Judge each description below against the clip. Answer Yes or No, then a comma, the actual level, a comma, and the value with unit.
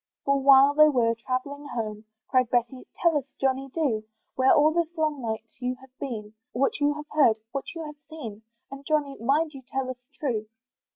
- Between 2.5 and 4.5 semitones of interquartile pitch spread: Yes, average, 3.2 semitones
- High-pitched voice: Yes, very high, 270 Hz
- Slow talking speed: No, average, 195 wpm